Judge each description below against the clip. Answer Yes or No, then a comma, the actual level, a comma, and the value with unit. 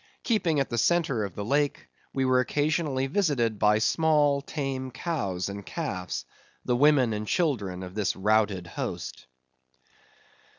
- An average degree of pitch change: No, wide, 6.2 semitones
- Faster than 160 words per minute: No, average, 140 wpm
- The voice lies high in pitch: No, low, 130 Hz